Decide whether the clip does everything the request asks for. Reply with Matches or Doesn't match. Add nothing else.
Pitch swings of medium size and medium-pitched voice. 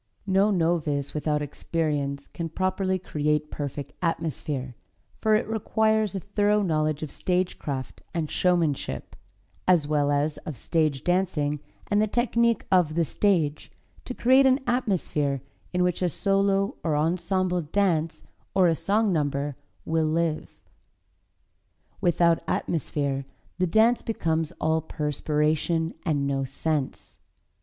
Matches